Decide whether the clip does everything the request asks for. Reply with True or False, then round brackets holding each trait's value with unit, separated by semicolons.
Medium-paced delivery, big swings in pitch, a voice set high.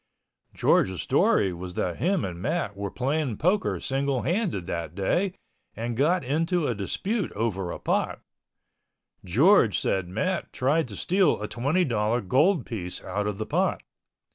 False (155 wpm; 9.0 semitones; 120 Hz)